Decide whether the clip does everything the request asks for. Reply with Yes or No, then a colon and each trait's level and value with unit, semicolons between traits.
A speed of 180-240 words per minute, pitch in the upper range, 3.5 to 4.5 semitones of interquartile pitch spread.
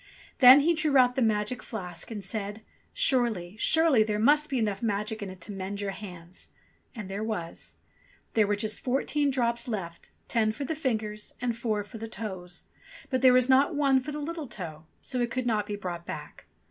Yes: average, 200 wpm; high, 220 Hz; average, 4.2 semitones